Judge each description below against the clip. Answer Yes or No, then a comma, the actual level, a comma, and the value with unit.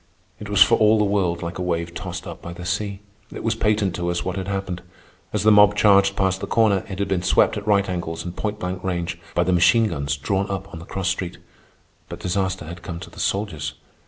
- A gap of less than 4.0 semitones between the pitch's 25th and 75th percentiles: Yes, average, 2.7 semitones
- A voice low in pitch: Yes, very low, 95 Hz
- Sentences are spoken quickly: Yes, fast, 245 wpm